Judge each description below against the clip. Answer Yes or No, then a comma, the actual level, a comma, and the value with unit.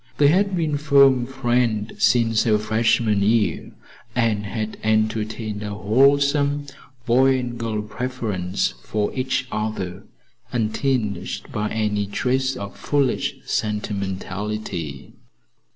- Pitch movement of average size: Yes, average, 3.7 semitones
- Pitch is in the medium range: No, low, 110 Hz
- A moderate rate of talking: No, slow, 105 wpm